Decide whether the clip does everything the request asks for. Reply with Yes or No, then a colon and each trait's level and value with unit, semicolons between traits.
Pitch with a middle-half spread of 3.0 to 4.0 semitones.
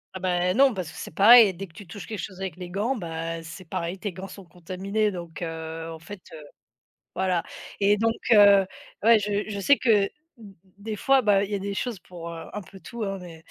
Yes: average, 3.3 semitones